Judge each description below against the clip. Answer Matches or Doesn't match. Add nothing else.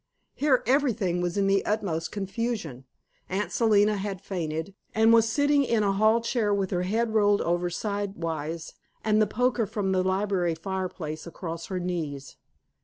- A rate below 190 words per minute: Matches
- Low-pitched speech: Doesn't match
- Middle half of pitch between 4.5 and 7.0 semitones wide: Doesn't match